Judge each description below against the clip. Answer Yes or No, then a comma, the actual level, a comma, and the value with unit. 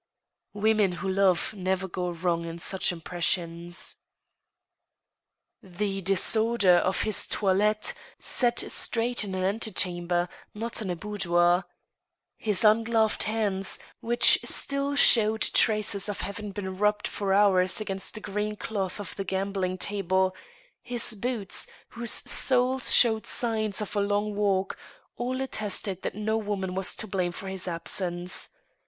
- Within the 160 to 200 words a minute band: No, slow, 135 wpm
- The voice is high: Yes, high, 200 Hz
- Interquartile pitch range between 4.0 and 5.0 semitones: No, average, 2.7 semitones